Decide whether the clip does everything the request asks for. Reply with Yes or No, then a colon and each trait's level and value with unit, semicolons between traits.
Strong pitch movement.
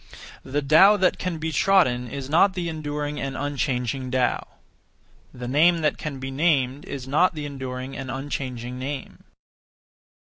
No: average, 3.2 semitones